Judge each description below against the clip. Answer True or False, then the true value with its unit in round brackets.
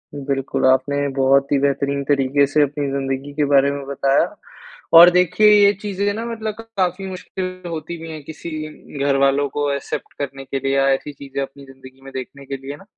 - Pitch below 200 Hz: True (140 Hz)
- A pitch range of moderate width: True (3.3 semitones)